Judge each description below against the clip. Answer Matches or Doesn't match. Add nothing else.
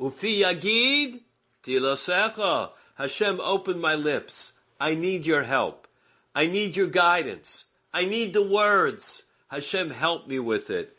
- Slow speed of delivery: Matches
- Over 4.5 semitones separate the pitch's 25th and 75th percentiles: Matches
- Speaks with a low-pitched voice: Doesn't match